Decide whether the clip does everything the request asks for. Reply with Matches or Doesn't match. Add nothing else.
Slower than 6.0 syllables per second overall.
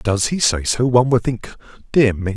Matches